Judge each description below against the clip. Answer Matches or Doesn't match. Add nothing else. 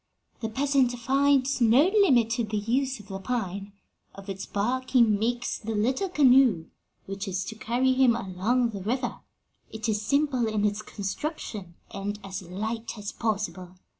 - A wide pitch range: Doesn't match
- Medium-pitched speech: Doesn't match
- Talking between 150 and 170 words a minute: Matches